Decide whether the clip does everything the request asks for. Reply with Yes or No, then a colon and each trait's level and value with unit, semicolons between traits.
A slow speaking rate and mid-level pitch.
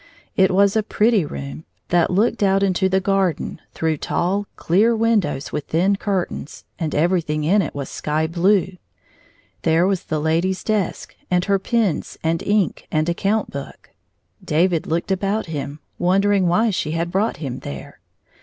No: average, 165 wpm; medium, 180 Hz